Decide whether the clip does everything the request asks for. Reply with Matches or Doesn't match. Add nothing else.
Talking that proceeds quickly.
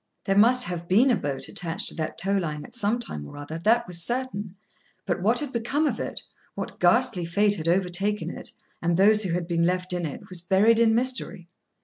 Matches